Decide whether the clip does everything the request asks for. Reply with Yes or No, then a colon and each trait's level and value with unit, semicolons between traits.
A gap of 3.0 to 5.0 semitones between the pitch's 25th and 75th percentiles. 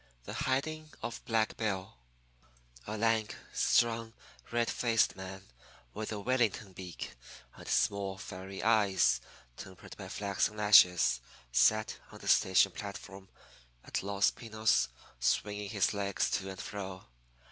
No: narrow, 2.6 semitones